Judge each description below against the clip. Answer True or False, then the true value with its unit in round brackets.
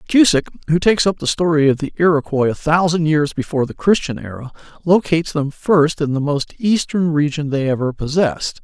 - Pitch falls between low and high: True (155 Hz)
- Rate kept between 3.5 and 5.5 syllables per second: False (5.8 syllables/s)